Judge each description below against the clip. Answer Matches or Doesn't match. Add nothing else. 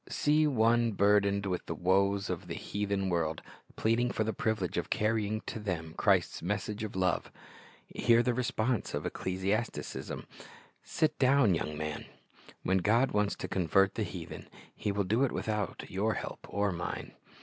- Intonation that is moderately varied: Matches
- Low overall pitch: Matches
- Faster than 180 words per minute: Doesn't match